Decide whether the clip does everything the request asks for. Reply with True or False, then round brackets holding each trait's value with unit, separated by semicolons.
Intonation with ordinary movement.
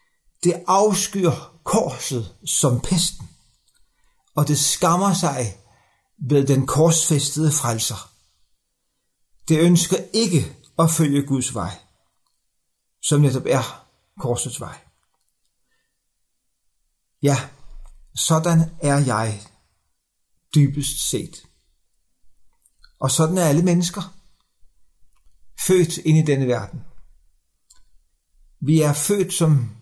False (6.1 semitones)